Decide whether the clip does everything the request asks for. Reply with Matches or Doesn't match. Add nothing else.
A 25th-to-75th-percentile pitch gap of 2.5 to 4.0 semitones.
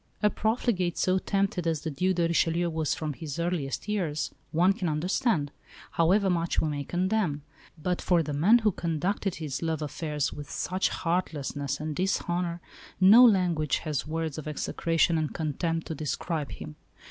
Matches